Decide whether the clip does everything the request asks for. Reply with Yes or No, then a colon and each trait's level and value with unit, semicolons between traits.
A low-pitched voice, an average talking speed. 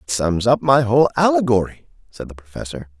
Yes: low, 105 Hz; average, 180 wpm